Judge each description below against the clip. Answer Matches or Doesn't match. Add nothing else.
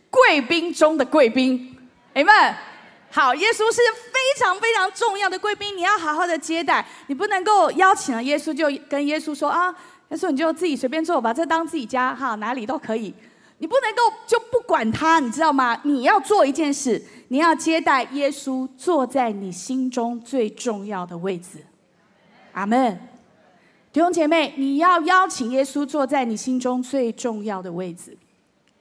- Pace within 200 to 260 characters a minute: Matches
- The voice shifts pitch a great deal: Matches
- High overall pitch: Matches